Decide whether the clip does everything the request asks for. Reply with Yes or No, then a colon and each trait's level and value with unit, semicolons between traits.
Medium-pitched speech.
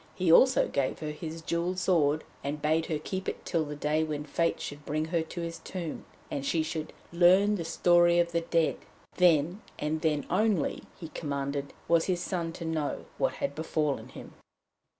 Yes: medium, 165 Hz